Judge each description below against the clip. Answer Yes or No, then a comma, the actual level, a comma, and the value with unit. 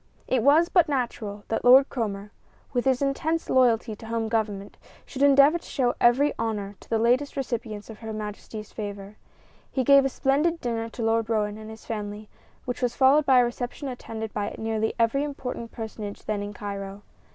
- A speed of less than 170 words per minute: No, average, 190 wpm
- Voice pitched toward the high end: Yes, high, 230 Hz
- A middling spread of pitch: Yes, average, 3.7 semitones